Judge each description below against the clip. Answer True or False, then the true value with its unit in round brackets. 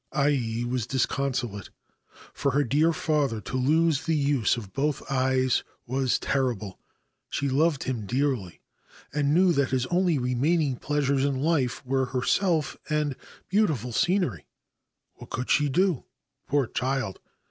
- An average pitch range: True (3.1 semitones)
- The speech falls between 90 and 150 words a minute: True (135 wpm)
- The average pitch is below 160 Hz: True (135 Hz)